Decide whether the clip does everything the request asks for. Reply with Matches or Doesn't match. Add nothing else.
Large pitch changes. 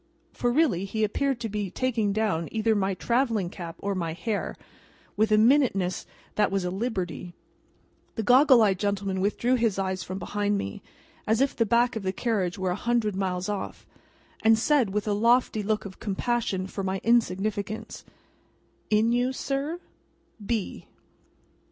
Doesn't match